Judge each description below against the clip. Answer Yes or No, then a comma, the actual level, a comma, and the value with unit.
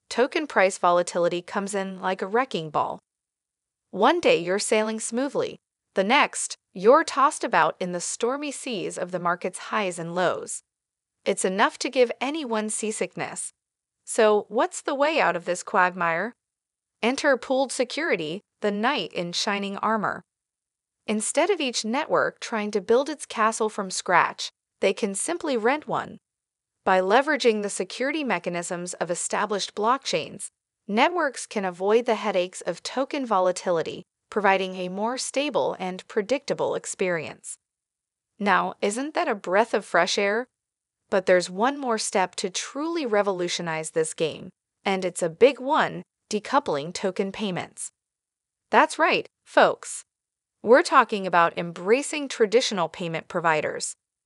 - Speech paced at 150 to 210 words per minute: No, average, 140 wpm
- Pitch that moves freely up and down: Yes, wide, 6.4 semitones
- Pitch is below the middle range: No, high, 220 Hz